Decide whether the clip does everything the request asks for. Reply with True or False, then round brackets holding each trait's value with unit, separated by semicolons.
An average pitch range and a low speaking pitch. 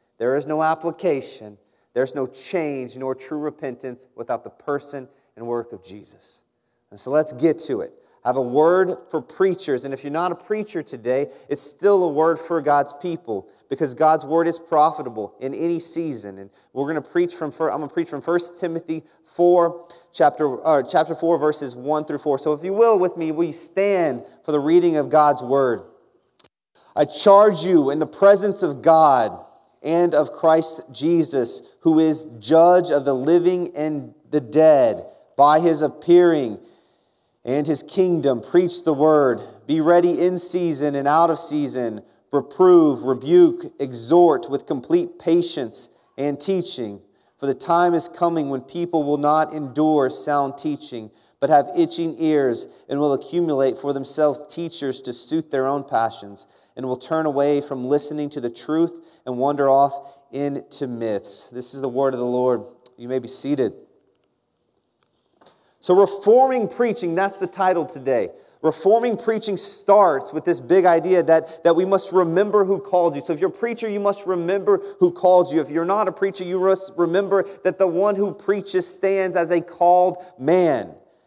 False (4.2 semitones; 160 Hz)